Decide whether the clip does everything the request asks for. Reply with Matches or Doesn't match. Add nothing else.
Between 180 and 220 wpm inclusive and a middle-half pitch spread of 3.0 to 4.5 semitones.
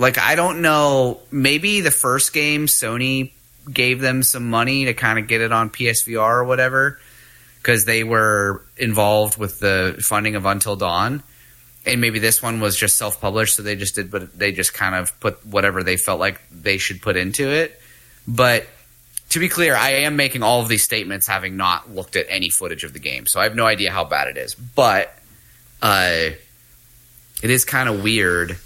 Matches